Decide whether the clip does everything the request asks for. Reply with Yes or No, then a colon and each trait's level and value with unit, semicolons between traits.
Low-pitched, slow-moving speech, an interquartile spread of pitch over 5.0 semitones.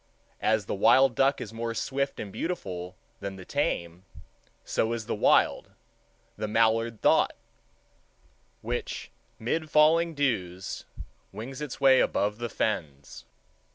Yes: low, 115 Hz; slow, 120 wpm; wide, 5.5 semitones